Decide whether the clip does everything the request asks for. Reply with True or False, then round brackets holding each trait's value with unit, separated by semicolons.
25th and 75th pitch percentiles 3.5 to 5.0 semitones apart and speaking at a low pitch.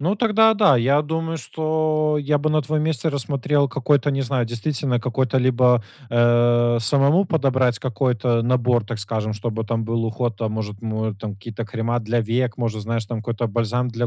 True (3.9 semitones; 120 Hz)